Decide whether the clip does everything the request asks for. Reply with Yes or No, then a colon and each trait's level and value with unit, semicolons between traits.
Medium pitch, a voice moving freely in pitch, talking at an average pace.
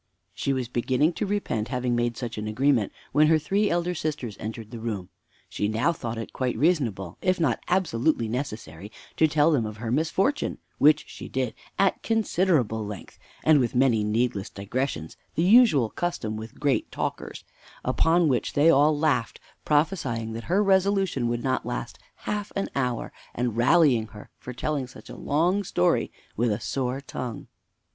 No: low, 130 Hz; wide, 6.0 semitones; average, 170 wpm